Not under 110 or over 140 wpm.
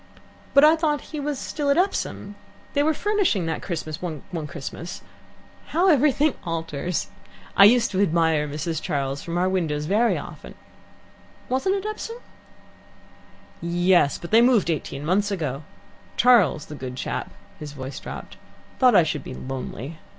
No: average, 150 wpm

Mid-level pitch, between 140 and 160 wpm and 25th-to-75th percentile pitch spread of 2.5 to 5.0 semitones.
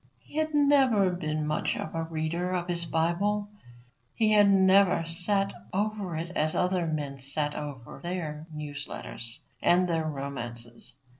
Yes: medium, 170 Hz; average, 145 wpm; average, 4.3 semitones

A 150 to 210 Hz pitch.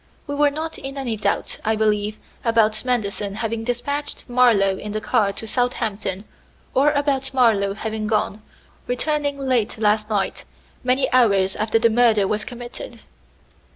No: high, 225 Hz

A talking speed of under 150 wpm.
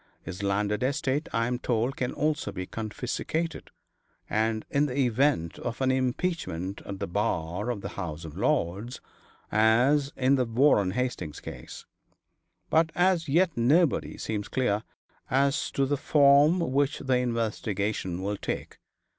Yes: average, 140 wpm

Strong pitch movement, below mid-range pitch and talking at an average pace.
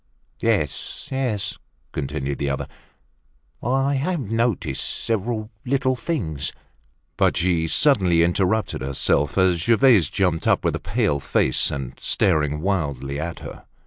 No: wide, 8.0 semitones; very low, 95 Hz; slow, 125 wpm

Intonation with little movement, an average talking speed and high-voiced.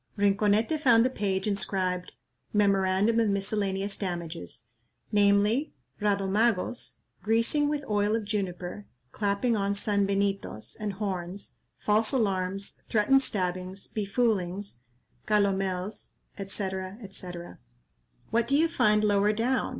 No: narrow, 2.1 semitones; slow, 110 wpm; high, 205 Hz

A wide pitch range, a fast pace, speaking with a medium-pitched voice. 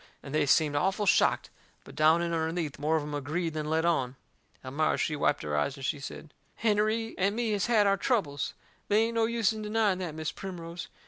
Yes: wide, 5.7 semitones; fast, 215 wpm; medium, 170 Hz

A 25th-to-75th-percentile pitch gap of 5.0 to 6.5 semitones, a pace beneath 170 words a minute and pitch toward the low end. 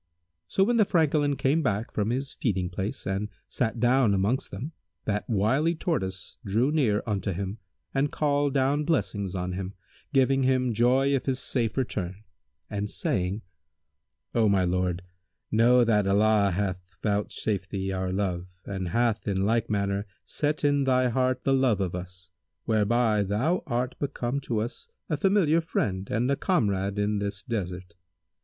Yes: average, 5.3 semitones; average, 160 wpm; low, 110 Hz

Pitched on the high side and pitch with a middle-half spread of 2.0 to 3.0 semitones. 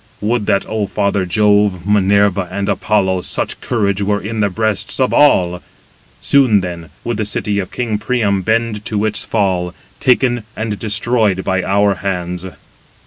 No: low, 105 Hz; narrow, 2.4 semitones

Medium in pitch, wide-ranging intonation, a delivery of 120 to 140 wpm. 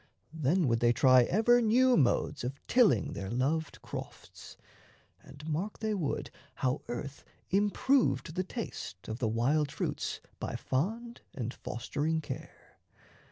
Yes: medium, 150 Hz; wide, 8.5 semitones; slow, 135 wpm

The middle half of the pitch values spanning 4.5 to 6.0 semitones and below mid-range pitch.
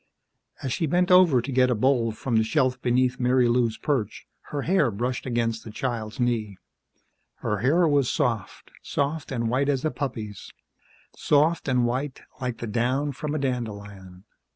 No: average, 3.4 semitones; low, 125 Hz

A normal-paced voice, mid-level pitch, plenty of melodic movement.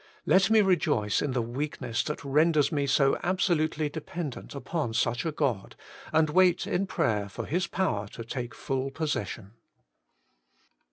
Yes: average, 160 wpm; medium, 145 Hz; wide, 5.8 semitones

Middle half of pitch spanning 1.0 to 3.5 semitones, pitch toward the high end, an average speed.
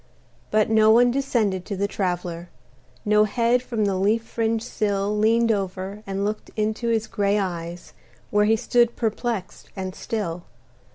Yes: average, 2.7 semitones; high, 210 Hz; average, 155 wpm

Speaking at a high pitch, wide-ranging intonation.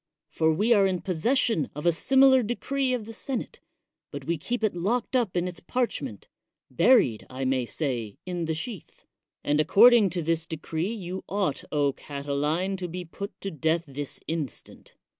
No: medium, 175 Hz; wide, 6.2 semitones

